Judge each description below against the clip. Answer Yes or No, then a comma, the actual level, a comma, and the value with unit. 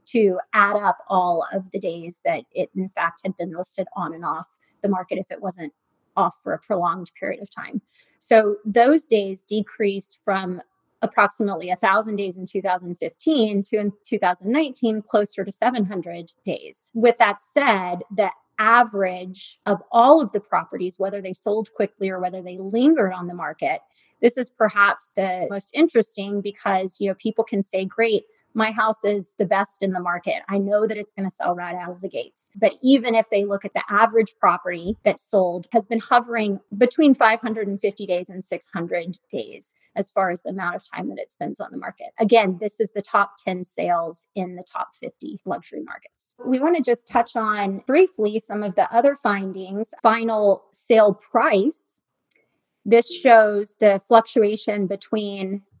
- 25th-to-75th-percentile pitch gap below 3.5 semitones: Yes, average, 3.0 semitones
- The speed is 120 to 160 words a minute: No, average, 180 wpm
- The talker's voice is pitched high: Yes, high, 205 Hz